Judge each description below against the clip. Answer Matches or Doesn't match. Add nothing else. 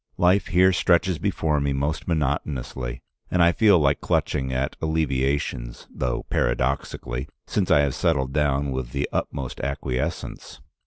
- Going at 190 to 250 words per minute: Doesn't match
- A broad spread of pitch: Doesn't match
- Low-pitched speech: Matches